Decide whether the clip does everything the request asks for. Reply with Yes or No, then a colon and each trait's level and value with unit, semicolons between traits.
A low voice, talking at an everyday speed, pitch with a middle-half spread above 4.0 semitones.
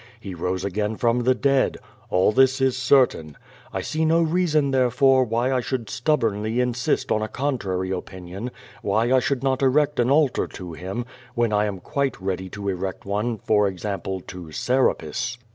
Yes: low, 120 Hz; average, 175 wpm; average, 5.3 semitones